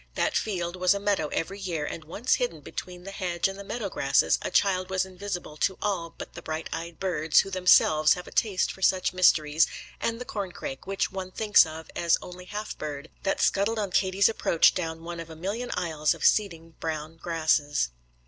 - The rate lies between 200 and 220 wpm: Yes, fast, 205 wpm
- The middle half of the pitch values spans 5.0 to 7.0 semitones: No, average, 3.3 semitones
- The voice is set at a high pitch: No, medium, 180 Hz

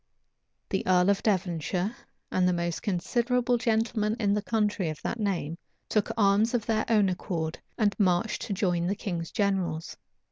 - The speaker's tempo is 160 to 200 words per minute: Yes, average, 165 wpm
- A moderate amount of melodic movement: Yes, average, 3.6 semitones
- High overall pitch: Yes, high, 200 Hz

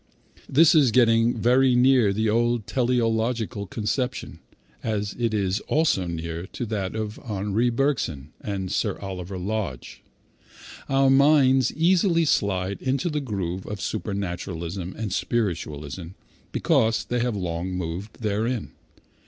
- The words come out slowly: Yes, slow, 130 wpm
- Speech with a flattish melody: No, average, 4.8 semitones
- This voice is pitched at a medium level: No, low, 110 Hz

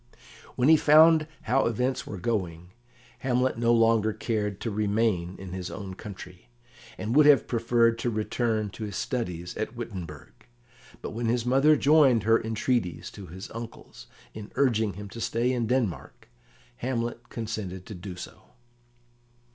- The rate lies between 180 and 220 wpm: No, average, 155 wpm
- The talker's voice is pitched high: No, low, 115 Hz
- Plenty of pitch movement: No, average, 3.7 semitones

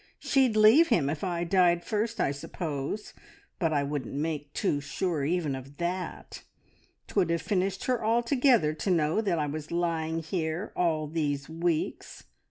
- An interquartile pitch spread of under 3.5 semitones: No, average, 4.3 semitones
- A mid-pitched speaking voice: Yes, medium, 170 Hz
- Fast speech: No, average, 160 wpm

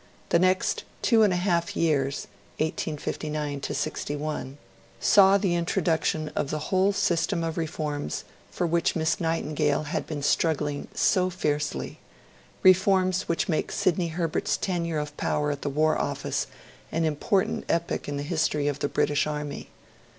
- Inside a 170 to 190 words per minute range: No, average, 145 wpm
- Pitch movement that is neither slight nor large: Yes, average, 3.0 semitones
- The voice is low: No, medium, 160 Hz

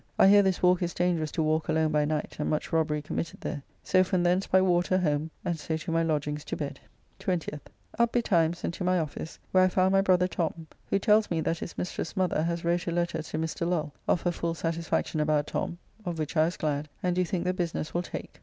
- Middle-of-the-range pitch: Yes, medium, 170 Hz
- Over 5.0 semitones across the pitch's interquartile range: No, narrow, 2.5 semitones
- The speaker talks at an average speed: No, fast, 240 wpm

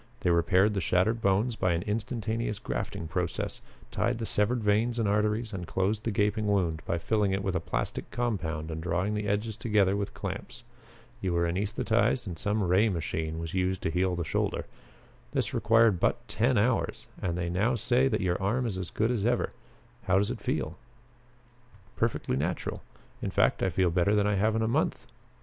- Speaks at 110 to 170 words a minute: No, average, 195 wpm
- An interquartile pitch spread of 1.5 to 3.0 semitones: No, average, 3.8 semitones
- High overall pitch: No, low, 100 Hz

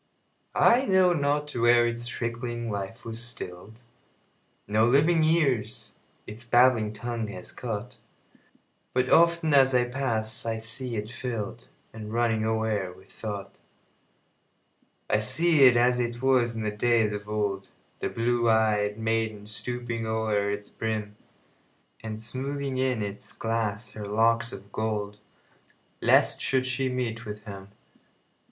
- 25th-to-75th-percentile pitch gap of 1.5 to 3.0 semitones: Yes, average, 2.7 semitones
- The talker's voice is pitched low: Yes, low, 115 Hz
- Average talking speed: No, slow, 120 wpm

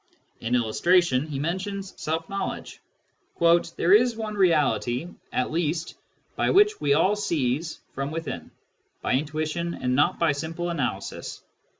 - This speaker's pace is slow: Yes, slow, 130 wpm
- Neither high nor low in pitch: Yes, medium, 165 Hz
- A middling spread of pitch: Yes, average, 4.4 semitones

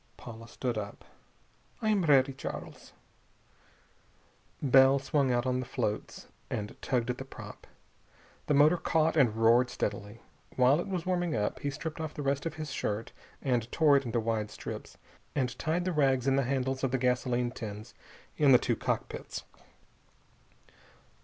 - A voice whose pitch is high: No, low, 130 Hz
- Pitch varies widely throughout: No, average, 3.4 semitones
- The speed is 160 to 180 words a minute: Yes, average, 165 wpm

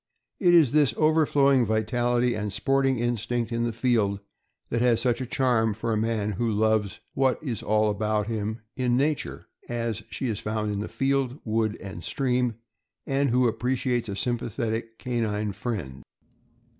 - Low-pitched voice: Yes, low, 115 Hz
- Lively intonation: No, average, 2.8 semitones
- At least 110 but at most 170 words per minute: Yes, average, 160 wpm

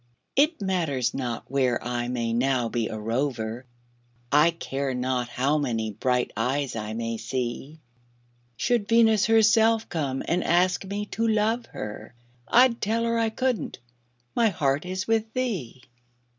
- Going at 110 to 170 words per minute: Yes, average, 145 wpm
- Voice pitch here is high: No, medium, 140 Hz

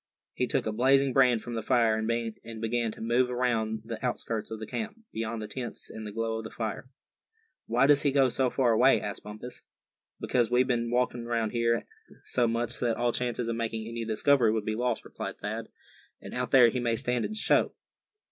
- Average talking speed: No, fast, 210 wpm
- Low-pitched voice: Yes, low, 115 Hz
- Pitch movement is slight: Yes, narrow, 1.9 semitones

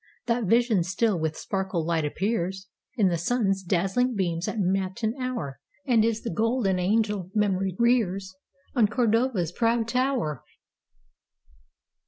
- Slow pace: Yes, slow, 115 wpm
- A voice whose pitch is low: No, high, 195 Hz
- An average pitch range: Yes, average, 4.1 semitones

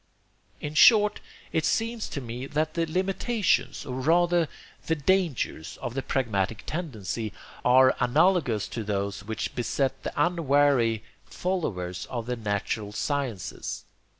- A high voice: No, low, 135 Hz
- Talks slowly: Yes, slow, 125 wpm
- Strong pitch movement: Yes, wide, 7.0 semitones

